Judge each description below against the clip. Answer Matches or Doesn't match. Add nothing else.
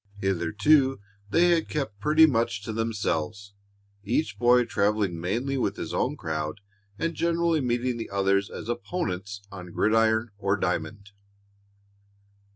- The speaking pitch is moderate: Doesn't match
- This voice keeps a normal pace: Doesn't match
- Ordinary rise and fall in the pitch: Matches